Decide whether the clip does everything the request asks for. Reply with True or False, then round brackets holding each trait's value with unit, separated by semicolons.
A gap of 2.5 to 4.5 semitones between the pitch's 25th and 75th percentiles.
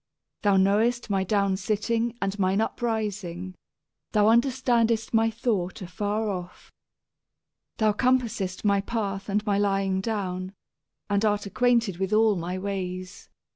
True (2.8 semitones)